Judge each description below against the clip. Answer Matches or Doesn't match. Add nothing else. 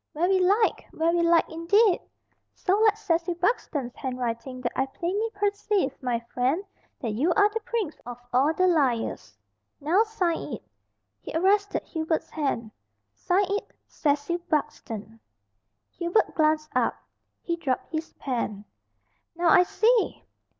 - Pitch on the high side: Matches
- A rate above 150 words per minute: Doesn't match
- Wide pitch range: Matches